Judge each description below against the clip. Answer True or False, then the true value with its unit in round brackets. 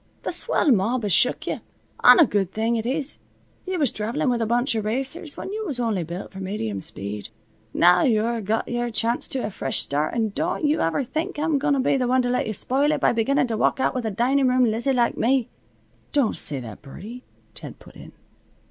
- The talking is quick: True (230 wpm)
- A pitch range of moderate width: True (4.3 semitones)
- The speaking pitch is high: True (240 Hz)